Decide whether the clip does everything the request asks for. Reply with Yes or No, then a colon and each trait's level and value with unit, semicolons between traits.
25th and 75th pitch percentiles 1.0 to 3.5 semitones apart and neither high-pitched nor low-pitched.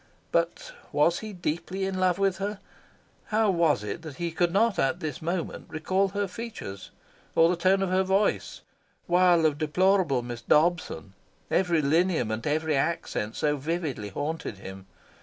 No: average, 4.2 semitones; medium, 170 Hz